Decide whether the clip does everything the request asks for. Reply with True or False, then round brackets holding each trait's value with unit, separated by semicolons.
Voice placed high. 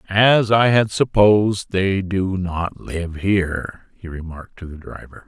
False (95 Hz)